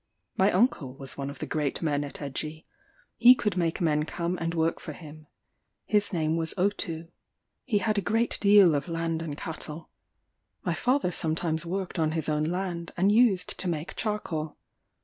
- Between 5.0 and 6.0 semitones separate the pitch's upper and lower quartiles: No, average, 3.7 semitones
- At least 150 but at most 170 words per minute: No, average, 180 wpm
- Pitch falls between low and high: Yes, medium, 165 Hz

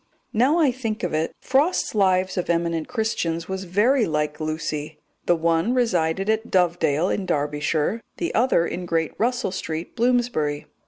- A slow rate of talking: No, average, 155 wpm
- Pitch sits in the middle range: Yes, medium, 180 Hz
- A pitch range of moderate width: No, wide, 6.0 semitones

